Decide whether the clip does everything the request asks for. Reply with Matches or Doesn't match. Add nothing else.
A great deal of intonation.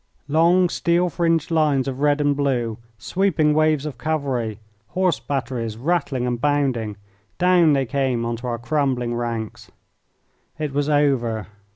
Doesn't match